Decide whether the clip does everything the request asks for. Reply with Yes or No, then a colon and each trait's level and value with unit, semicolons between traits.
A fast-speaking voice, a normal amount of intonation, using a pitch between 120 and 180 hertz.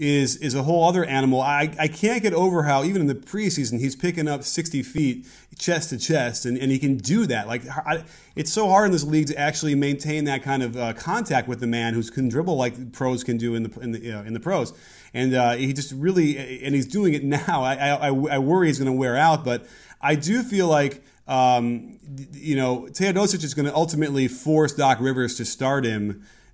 Yes: fast, 235 wpm; average, 3.6 semitones; medium, 140 Hz